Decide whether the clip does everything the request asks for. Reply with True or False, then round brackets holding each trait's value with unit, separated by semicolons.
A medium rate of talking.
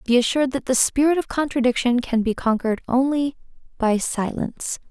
True (160 wpm)